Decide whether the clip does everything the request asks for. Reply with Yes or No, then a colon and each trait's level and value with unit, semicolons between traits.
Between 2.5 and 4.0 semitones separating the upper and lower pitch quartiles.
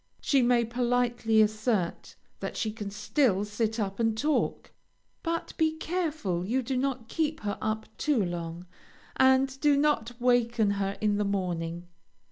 No: average, 4.4 semitones